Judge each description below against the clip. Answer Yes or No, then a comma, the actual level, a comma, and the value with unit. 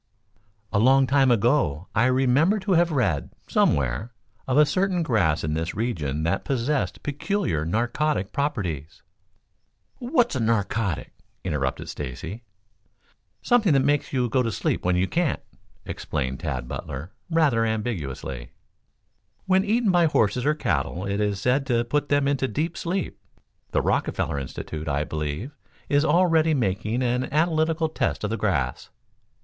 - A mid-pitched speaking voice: No, low, 120 Hz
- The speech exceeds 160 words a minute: No, average, 145 wpm